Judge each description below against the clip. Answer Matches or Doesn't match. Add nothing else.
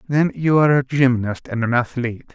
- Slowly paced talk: Doesn't match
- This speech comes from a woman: Doesn't match